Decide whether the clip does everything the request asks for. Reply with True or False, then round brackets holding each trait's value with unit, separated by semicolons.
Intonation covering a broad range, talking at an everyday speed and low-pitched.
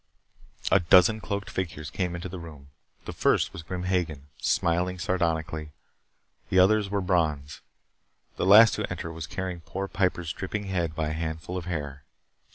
False (2.8 semitones; 165 wpm; 90 Hz)